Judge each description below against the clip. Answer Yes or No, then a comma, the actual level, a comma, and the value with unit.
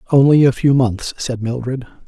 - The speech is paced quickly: No, average, 175 wpm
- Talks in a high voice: No, low, 130 Hz